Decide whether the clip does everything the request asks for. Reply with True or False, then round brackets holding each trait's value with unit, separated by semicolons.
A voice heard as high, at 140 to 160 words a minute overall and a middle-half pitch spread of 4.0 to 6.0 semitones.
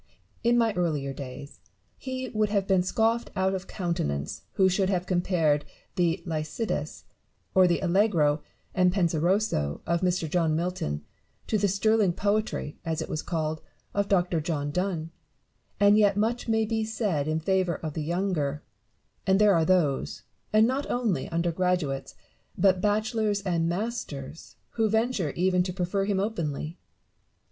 False (180 Hz; 155 wpm; 4.3 semitones)